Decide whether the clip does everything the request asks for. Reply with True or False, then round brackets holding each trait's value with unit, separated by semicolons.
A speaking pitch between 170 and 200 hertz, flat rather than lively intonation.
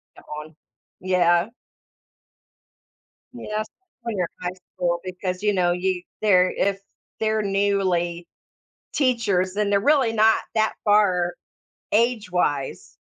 False (190 Hz; 3.2 semitones)